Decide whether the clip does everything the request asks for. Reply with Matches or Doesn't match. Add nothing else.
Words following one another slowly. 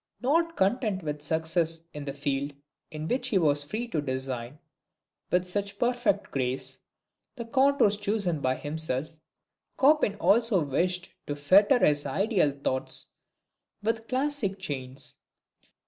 Matches